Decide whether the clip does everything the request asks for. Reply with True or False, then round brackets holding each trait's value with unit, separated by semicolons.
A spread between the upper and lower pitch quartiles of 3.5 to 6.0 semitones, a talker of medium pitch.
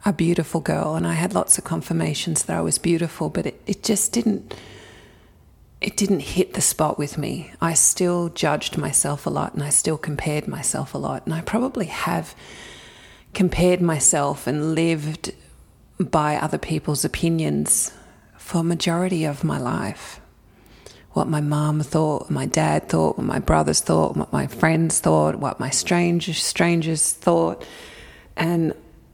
False (2.8 semitones; 160 Hz)